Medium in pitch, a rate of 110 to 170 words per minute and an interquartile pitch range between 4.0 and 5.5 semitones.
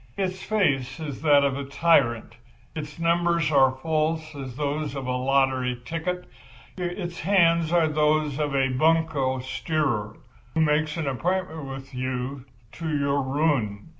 No: medium, 150 Hz; average, 145 wpm; average, 3.5 semitones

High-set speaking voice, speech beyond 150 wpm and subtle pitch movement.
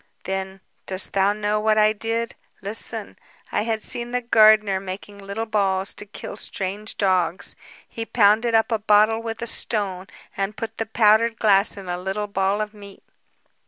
Yes: high, 210 Hz; average, 170 wpm; narrow, 2.3 semitones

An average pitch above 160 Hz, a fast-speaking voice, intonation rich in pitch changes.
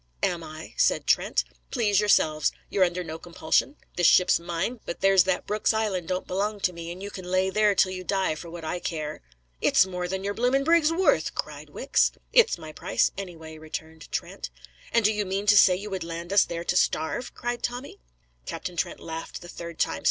No: medium, 185 Hz; fast, 210 wpm; average, 3.5 semitones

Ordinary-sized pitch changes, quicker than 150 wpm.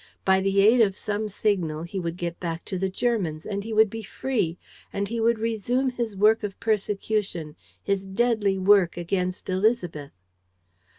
Yes: average, 3.2 semitones; average, 170 wpm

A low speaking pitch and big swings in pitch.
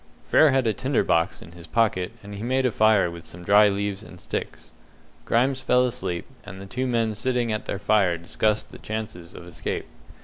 No: low, 105 Hz; average, 4.7 semitones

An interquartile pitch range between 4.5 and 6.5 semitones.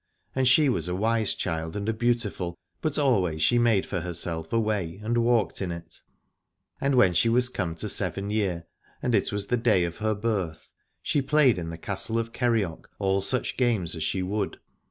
Yes: average, 5.2 semitones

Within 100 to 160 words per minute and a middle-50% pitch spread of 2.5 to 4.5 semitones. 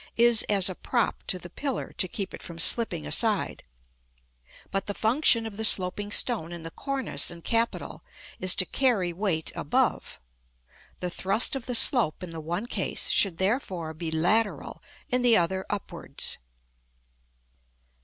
No: average, 155 wpm; average, 5.0 semitones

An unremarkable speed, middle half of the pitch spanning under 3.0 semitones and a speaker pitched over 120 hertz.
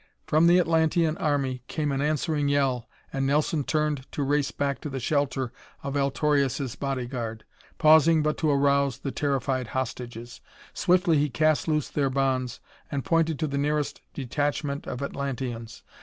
Yes: average, 155 wpm; narrow, 2.4 semitones; medium, 140 Hz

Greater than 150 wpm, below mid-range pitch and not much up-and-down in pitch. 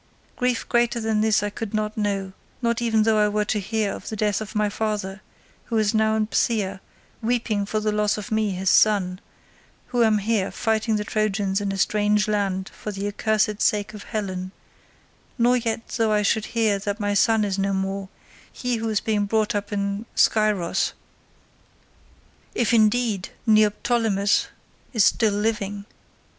No: average, 170 wpm; high, 210 Hz; narrow, 1.6 semitones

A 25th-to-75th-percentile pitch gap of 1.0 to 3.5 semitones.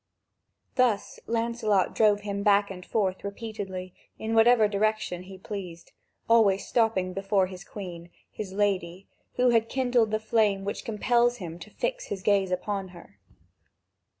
Yes: average, 2.9 semitones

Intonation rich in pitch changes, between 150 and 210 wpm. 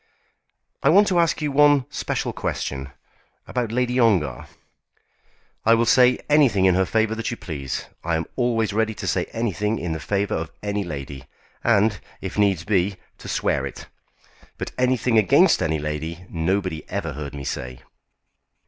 Yes: wide, 6.5 semitones; average, 165 wpm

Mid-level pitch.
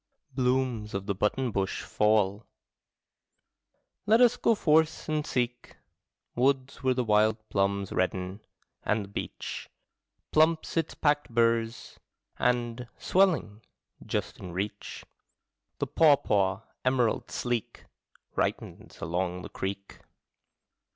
No: low, 115 Hz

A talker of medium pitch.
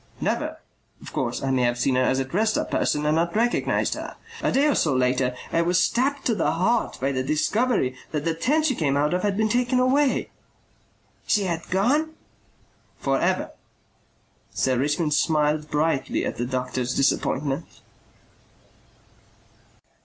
Yes: medium, 160 Hz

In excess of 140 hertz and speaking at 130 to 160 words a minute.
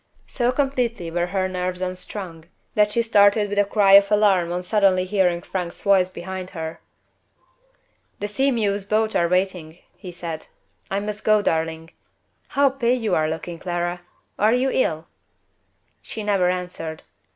Yes: high, 190 Hz; average, 155 wpm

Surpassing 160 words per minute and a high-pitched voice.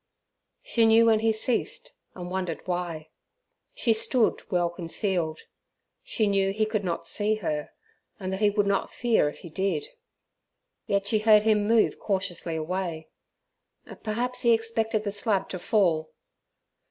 No: average, 150 wpm; high, 200 Hz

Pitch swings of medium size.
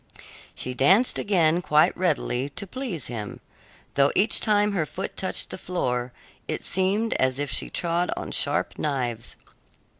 No: wide, 6.9 semitones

